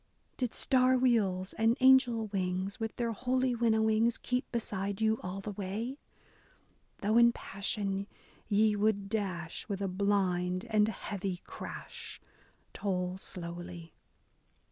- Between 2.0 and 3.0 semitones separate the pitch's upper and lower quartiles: No, average, 3.4 semitones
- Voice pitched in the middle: No, high, 205 Hz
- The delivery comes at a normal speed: No, slow, 120 wpm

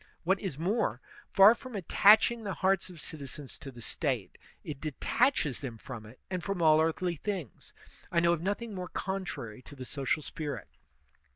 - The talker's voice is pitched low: No, medium, 170 Hz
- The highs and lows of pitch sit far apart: Yes, wide, 5.9 semitones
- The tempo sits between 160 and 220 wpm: Yes, average, 175 wpm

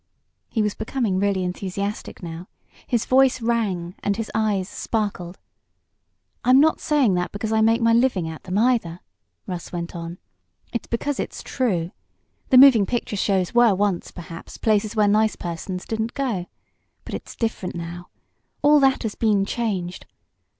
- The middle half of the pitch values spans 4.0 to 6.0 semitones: Yes, average, 4.4 semitones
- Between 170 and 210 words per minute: No, average, 155 wpm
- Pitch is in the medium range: No, high, 210 Hz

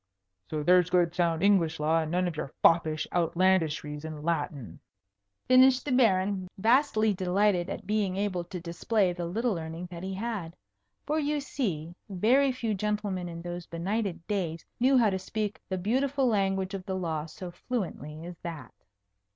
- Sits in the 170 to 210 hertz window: Yes, medium, 185 Hz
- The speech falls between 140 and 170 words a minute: Yes, average, 165 wpm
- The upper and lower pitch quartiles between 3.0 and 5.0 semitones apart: Yes, average, 4.1 semitones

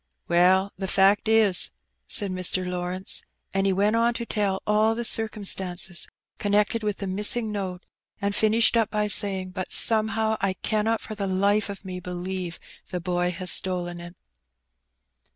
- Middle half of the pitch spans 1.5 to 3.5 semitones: Yes, average, 2.7 semitones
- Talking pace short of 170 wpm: Yes, average, 160 wpm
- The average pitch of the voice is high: Yes, high, 195 Hz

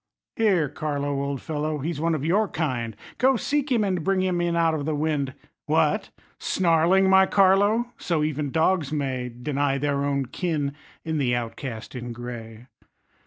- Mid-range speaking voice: Yes, medium, 155 Hz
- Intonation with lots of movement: No, average, 4.9 semitones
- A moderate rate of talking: Yes, average, 165 wpm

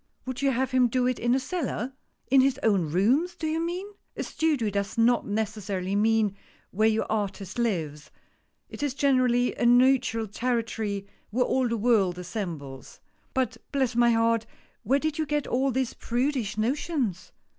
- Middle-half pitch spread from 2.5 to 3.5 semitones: No, average, 4.1 semitones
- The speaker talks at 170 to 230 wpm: Yes, average, 175 wpm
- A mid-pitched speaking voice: No, high, 235 Hz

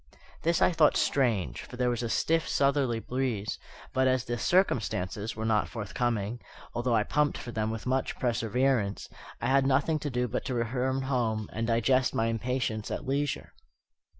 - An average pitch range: Yes, average, 3.0 semitones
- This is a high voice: No, low, 125 Hz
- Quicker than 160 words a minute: Yes, average, 175 wpm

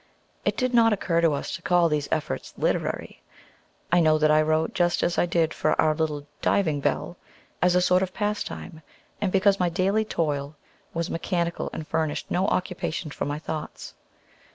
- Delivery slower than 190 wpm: Yes, average, 180 wpm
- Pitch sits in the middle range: Yes, medium, 170 Hz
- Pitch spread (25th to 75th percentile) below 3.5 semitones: Yes, average, 2.9 semitones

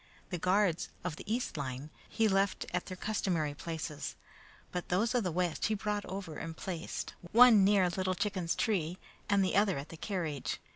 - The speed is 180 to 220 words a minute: Yes, average, 185 wpm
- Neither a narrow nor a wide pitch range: Yes, average, 3.8 semitones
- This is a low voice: No, medium, 185 Hz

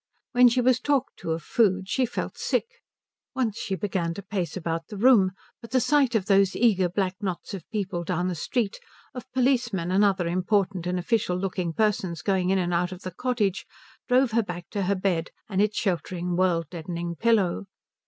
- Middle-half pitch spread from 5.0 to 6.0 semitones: No, average, 4.2 semitones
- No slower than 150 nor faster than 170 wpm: No, average, 195 wpm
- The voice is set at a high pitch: Yes, high, 195 Hz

